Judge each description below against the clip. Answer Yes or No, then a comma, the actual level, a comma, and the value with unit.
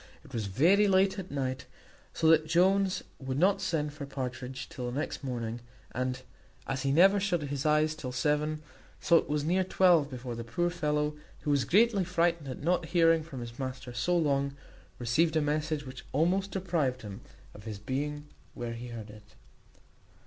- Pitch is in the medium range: Yes, medium, 150 Hz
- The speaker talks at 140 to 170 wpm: No, average, 185 wpm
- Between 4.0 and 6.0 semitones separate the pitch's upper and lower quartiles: Yes, average, 4.8 semitones